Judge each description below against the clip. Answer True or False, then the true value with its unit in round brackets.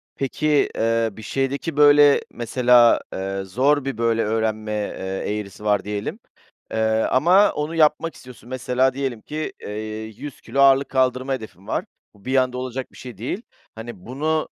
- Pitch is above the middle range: False (125 Hz)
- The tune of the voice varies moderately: True (4.1 semitones)